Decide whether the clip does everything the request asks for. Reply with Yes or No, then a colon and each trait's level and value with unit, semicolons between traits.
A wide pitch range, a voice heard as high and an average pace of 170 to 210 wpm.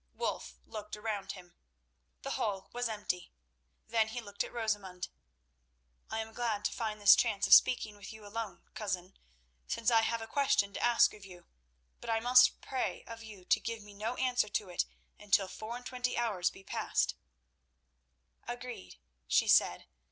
No: average, 2.7 semitones; high, 215 Hz; average, 175 wpm